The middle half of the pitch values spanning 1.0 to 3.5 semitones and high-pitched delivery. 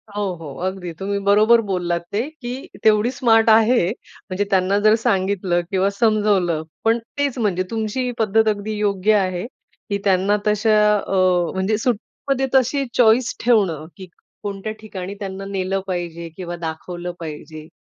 Yes: average, 3.2 semitones; high, 200 Hz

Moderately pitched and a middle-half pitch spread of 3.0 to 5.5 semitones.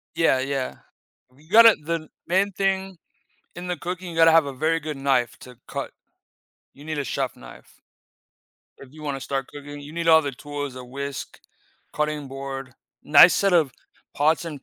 Yes: medium, 150 Hz; average, 3.3 semitones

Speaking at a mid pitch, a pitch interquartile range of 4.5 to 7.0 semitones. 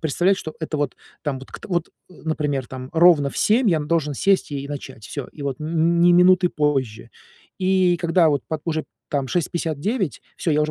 No: medium, 155 Hz; average, 3.7 semitones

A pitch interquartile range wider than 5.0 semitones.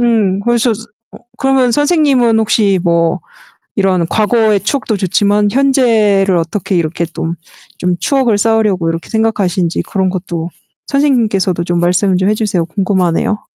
No: average, 4.1 semitones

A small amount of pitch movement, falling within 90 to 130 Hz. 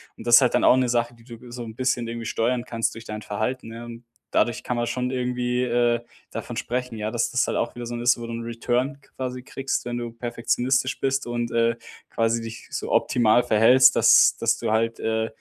Yes: narrow, 1.4 semitones; low, 120 Hz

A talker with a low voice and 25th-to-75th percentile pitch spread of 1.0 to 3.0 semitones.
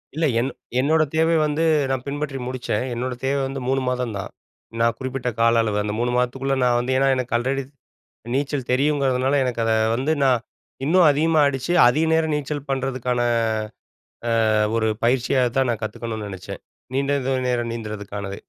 Yes: low, 130 Hz; average, 2.7 semitones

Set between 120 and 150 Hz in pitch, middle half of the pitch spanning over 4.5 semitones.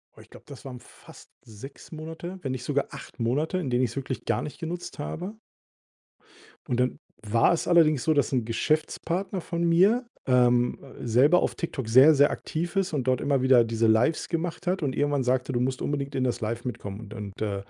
Yes: low, 135 Hz; average, 5.0 semitones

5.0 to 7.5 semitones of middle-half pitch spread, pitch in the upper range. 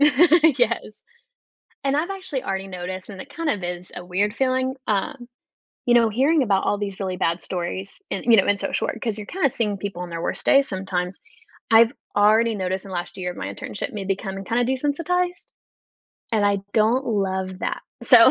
Yes: wide, 5.5 semitones; high, 210 Hz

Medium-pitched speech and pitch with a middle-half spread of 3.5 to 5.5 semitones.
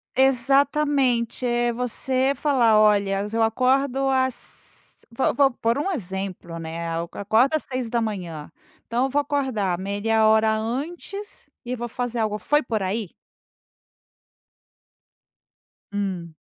No: high, 235 Hz; average, 4.4 semitones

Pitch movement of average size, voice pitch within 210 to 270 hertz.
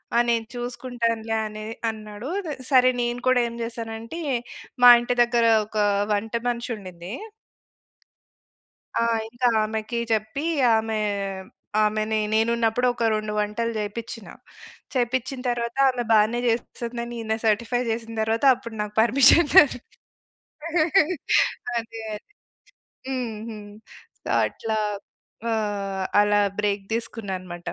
No: narrow, 2.0 semitones; high, 225 Hz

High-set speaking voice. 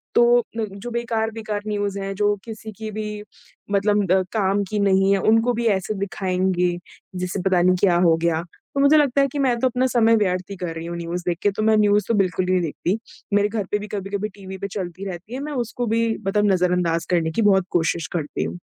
Yes: high, 200 Hz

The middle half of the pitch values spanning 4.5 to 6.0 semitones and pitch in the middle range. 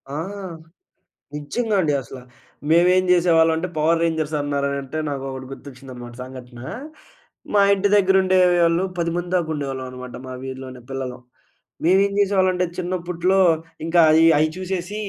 Yes: average, 5.2 semitones; medium, 165 Hz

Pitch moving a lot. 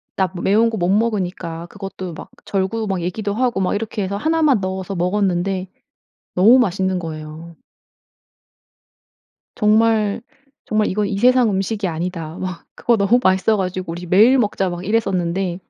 No: average, 3.1 semitones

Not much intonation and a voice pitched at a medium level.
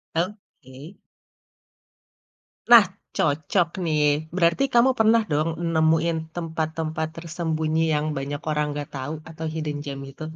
Yes: narrow, 2.1 semitones; medium, 160 Hz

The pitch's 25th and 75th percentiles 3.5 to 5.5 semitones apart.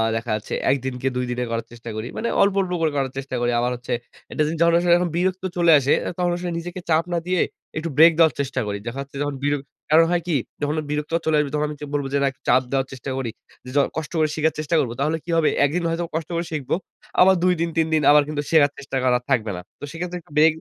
Yes: average, 4.0 semitones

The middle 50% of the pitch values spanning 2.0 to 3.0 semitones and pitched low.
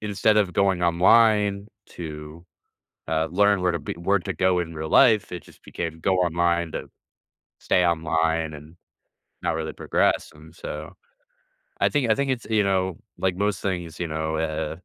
No: average, 3.6 semitones; very low, 85 Hz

